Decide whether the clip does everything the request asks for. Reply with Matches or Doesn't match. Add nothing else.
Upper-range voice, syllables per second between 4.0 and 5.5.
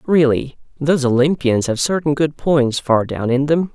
Doesn't match